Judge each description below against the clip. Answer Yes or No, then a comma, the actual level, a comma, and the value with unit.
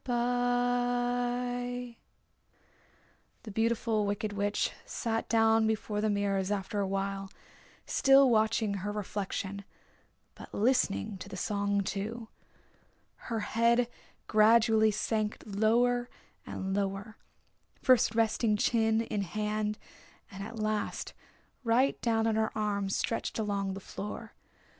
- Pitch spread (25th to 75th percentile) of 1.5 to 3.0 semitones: Yes, narrow, 2.5 semitones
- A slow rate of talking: Yes, slow, 110 wpm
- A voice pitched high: Yes, high, 220 Hz